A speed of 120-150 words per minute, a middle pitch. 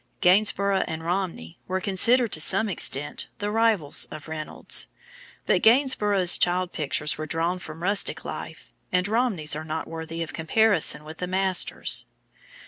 Yes: average, 145 wpm; medium, 180 Hz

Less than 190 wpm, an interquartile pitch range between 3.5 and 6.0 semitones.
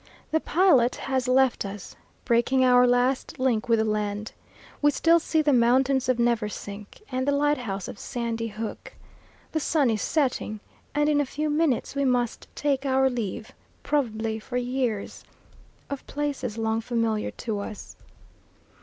Yes: average, 155 wpm; average, 3.8 semitones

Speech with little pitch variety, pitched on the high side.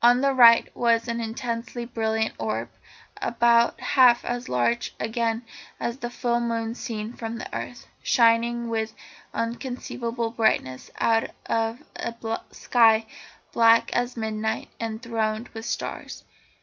Yes: narrow, 1.2 semitones; high, 230 Hz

